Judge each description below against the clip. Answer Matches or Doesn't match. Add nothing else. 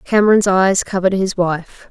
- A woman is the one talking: Matches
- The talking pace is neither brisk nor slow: Matches